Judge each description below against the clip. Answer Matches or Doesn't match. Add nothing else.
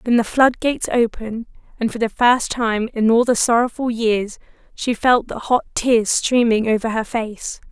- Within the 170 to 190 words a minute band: Matches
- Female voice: Matches